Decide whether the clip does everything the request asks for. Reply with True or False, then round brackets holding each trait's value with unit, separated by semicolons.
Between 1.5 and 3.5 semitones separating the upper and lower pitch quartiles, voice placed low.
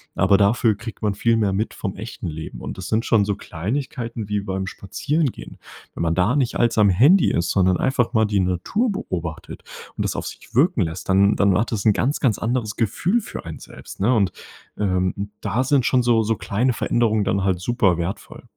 False (4.0 semitones; 105 Hz)